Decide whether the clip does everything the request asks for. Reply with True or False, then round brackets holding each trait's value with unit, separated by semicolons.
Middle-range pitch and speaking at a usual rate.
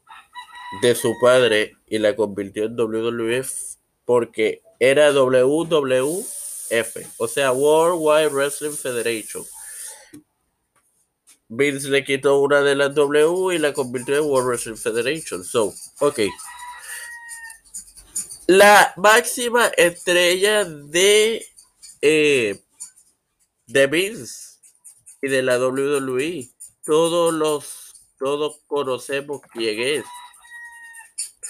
False (150 Hz; 95 wpm)